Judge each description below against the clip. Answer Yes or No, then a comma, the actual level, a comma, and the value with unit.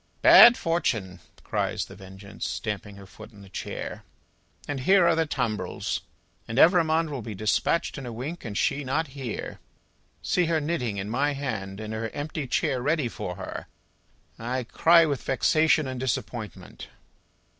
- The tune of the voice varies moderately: No, wide, 6.4 semitones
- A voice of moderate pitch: No, low, 130 Hz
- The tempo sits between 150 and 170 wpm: Yes, average, 160 wpm